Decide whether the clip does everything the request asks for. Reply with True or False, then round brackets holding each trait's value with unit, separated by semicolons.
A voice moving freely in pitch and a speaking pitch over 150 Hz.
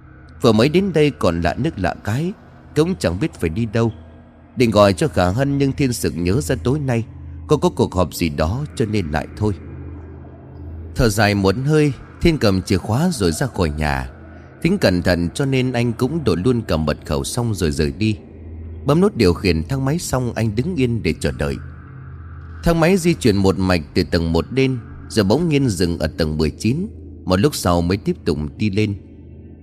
False (8.0 semitones; 95 Hz)